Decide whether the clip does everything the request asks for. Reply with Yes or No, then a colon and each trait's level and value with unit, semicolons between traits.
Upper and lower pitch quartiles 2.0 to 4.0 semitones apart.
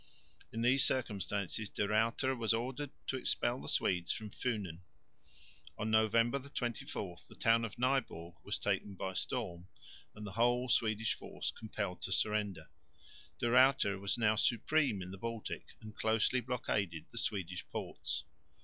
Yes: average, 3.4 semitones